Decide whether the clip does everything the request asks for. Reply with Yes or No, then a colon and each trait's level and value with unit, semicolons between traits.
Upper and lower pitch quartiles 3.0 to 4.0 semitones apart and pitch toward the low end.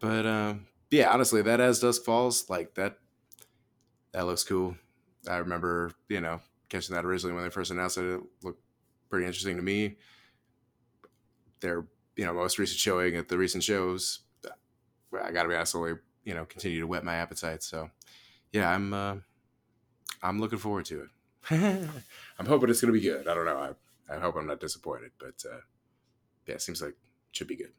No: average, 4.8 semitones; very low, 95 Hz